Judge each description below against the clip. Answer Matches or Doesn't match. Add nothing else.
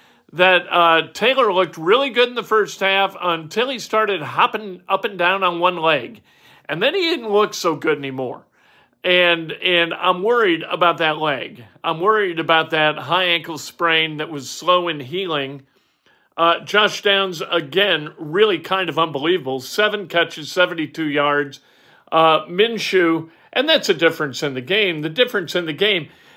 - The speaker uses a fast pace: Doesn't match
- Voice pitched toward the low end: Doesn't match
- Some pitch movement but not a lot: Matches